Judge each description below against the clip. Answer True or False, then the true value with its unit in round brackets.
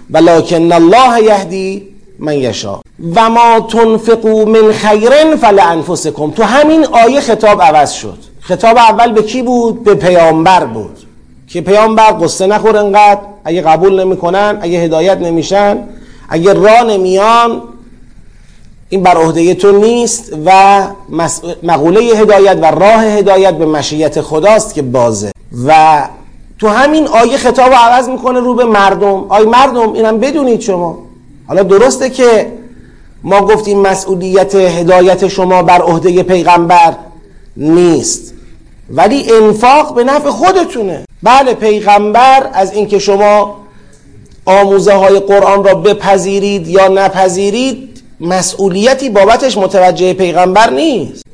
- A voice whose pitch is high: True (200 Hz)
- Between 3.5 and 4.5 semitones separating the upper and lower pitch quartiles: True (3.9 semitones)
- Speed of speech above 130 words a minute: False (125 wpm)